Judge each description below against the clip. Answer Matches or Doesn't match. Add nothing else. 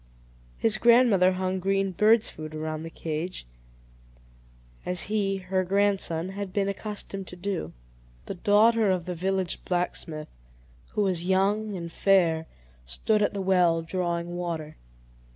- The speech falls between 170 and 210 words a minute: Doesn't match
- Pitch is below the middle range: Doesn't match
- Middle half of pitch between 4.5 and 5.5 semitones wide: Doesn't match